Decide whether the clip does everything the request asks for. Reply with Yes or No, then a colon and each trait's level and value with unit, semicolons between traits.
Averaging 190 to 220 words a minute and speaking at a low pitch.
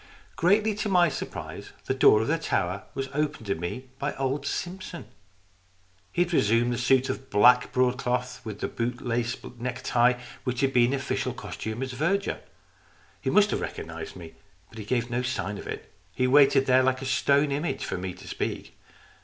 Yes: average, 195 wpm; low, 125 Hz